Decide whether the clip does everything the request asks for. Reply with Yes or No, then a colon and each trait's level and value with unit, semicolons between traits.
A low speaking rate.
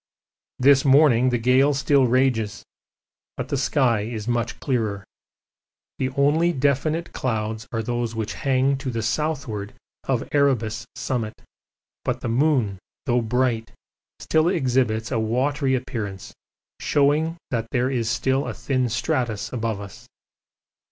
Yes: slow, 130 wpm